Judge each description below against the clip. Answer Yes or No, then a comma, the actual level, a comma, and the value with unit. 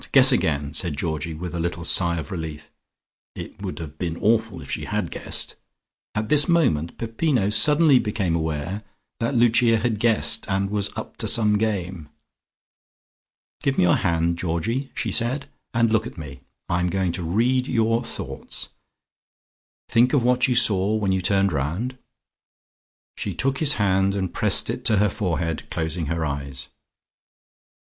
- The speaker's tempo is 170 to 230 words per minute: No, average, 160 wpm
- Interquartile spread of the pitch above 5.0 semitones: Yes, wide, 5.6 semitones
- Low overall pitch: Yes, very low, 95 Hz